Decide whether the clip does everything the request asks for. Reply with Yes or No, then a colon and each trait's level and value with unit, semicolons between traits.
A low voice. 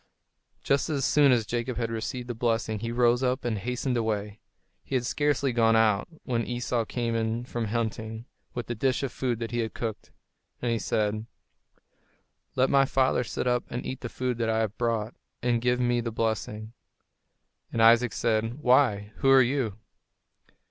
Yes: low, 120 Hz